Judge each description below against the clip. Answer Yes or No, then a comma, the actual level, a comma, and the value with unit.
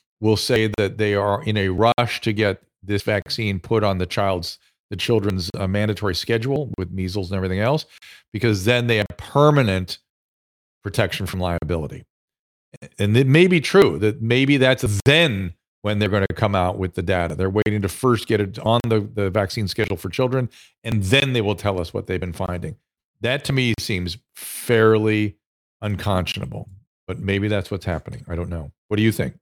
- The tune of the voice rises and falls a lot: No, average, 3.4 semitones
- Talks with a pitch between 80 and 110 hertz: Yes, low, 105 Hz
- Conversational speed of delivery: Yes, average, 190 wpm